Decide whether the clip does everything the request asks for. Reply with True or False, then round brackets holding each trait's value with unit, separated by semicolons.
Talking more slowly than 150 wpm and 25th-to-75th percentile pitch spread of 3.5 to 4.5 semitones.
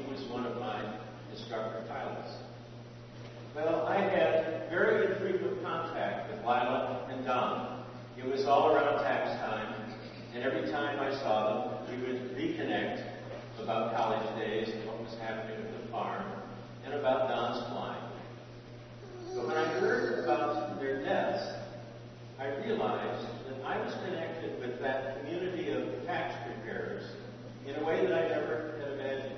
False (140 wpm; 2.8 semitones)